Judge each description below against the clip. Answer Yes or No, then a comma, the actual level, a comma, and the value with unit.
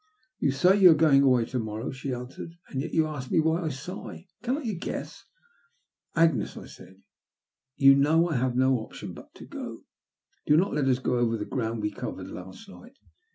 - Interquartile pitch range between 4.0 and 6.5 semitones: Yes, average, 5.0 semitones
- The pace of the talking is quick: Yes, fast, 220 wpm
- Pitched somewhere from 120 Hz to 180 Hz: Yes, medium, 140 Hz